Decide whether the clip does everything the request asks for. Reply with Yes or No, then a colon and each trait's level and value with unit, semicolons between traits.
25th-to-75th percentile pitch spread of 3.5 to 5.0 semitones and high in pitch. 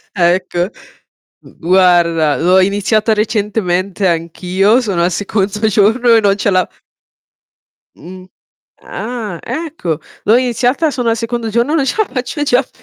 Yes: average, 4.6 semitones; high, 205 Hz